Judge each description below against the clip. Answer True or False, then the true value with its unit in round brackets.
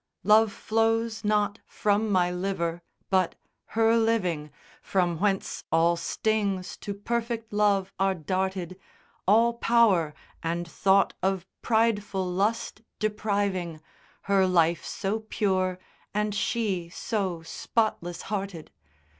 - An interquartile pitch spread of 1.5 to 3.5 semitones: True (3.2 semitones)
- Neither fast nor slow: False (115 wpm)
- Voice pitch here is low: False (195 Hz)